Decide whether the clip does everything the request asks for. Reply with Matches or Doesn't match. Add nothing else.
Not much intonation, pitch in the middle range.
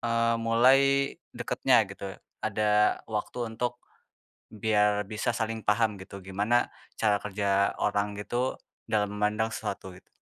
Doesn't match